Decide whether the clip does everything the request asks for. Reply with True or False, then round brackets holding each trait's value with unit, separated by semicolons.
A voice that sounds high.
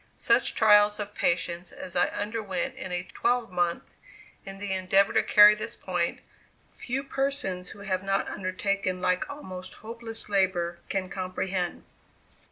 True (195 Hz)